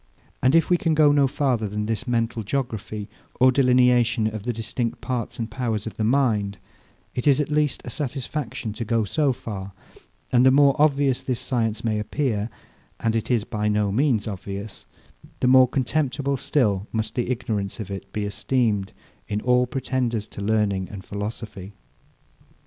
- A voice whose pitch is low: Yes, low, 115 Hz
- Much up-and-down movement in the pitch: No, average, 3.7 semitones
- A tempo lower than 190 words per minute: Yes, average, 170 wpm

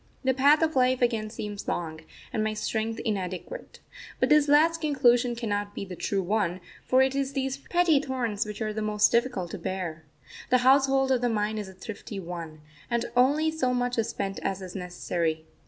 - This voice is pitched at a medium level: No, high, 225 Hz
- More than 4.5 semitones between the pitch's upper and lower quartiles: Yes, average, 5.1 semitones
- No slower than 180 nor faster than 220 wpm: Yes, average, 195 wpm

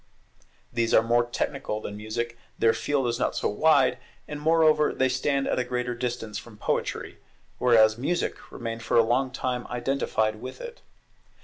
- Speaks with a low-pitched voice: Yes, low, 120 Hz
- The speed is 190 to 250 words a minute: No, average, 170 wpm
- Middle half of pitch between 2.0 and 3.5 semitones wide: Yes, average, 2.9 semitones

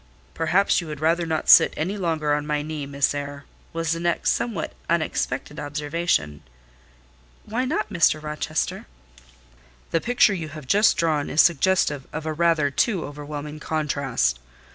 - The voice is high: No, medium, 155 Hz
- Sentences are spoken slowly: No, average, 150 wpm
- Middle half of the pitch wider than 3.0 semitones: No, narrow, 2.5 semitones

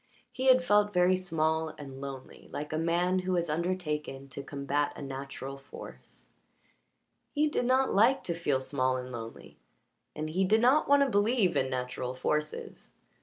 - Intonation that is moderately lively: No, wide, 6.7 semitones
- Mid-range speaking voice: Yes, medium, 160 Hz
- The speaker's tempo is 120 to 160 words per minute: No, average, 170 wpm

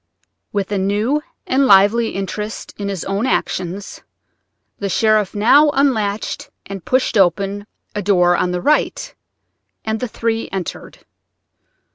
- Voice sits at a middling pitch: No, high, 205 Hz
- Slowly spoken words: Yes, slow, 130 wpm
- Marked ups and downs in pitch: No, average, 2.7 semitones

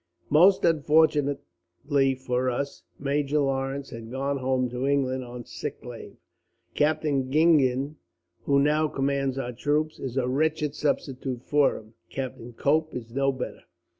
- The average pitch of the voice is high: No, low, 135 Hz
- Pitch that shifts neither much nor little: No, narrow, 2.3 semitones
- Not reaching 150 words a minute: Yes, slow, 135 wpm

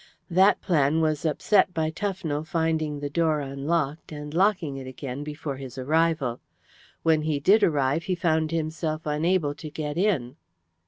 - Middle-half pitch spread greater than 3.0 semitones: No, narrow, 2.5 semitones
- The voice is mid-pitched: Yes, medium, 155 Hz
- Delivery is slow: No, average, 155 wpm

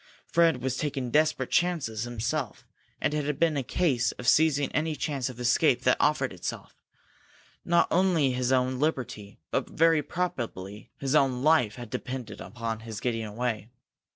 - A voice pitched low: Yes, low, 130 Hz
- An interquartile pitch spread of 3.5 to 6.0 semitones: Yes, average, 4.5 semitones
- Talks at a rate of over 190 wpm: No, average, 160 wpm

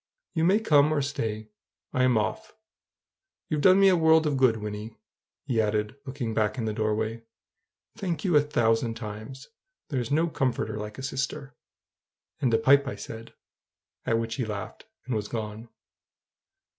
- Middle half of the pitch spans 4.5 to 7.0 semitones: Yes, average, 4.8 semitones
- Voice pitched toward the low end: Yes, low, 125 Hz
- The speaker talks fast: No, average, 155 wpm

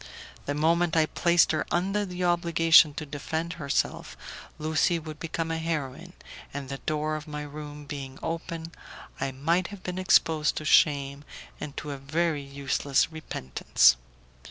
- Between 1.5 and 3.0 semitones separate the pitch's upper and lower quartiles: Yes, average, 2.7 semitones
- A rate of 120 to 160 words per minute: Yes, average, 155 wpm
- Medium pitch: Yes, medium, 155 Hz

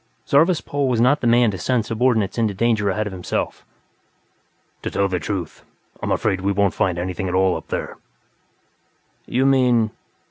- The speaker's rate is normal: Yes, average, 175 wpm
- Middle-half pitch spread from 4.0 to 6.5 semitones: Yes, average, 4.4 semitones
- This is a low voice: Yes, low, 110 Hz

